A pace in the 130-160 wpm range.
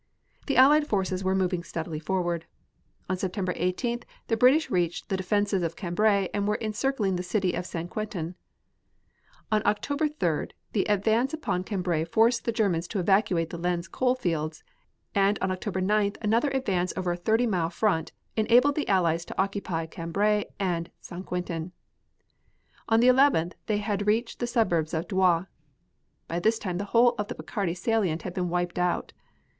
No: average, 170 wpm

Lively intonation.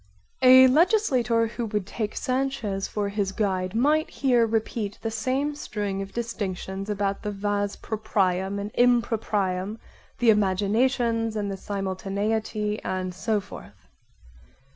No: average, 3.2 semitones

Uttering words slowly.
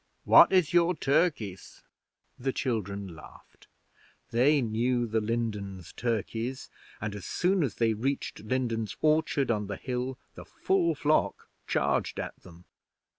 Yes: slow, 130 wpm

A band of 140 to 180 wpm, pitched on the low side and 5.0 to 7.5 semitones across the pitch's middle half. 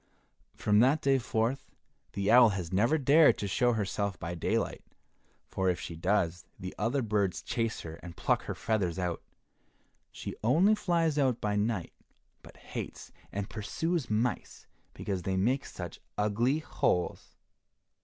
Yes: average, 150 wpm; low, 105 Hz; wide, 5.5 semitones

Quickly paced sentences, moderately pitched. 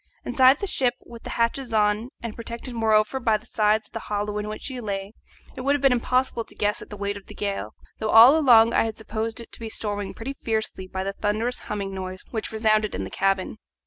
No: fast, 240 wpm; high, 220 Hz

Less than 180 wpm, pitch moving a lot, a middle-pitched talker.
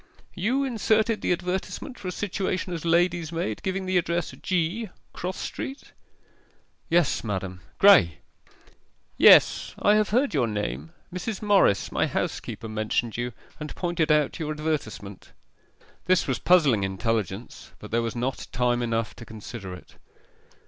Yes: average, 140 wpm; wide, 8.5 semitones; medium, 160 Hz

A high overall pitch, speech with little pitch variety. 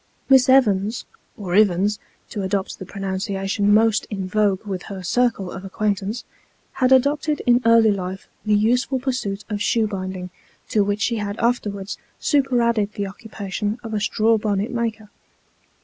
No: high, 210 Hz; average, 3.0 semitones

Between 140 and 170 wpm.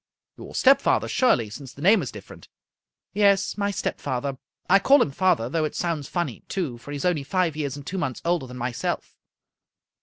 No: fast, 205 wpm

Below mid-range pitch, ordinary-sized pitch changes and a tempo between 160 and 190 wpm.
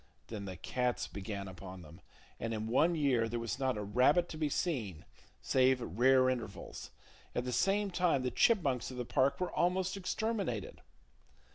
No: low, 125 Hz; wide, 7.1 semitones; average, 175 wpm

